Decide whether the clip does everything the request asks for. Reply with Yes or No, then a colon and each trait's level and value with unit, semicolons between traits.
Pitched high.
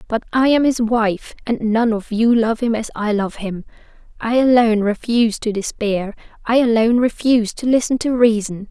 Yes: high, 225 Hz